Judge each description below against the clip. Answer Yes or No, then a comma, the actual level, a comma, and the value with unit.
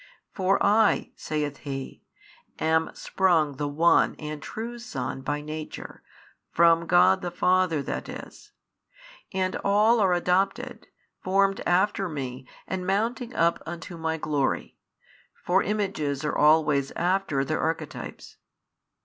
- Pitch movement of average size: Yes, average, 4.1 semitones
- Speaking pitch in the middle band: Yes, medium, 170 Hz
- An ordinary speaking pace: No, slow, 125 wpm